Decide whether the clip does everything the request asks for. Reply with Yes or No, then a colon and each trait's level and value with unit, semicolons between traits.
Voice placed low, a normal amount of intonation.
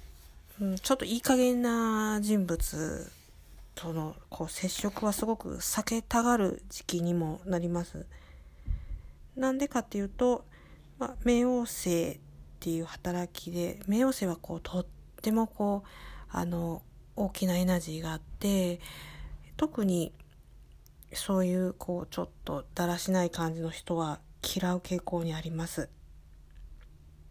No: medium, 175 Hz; average, 4.4 semitones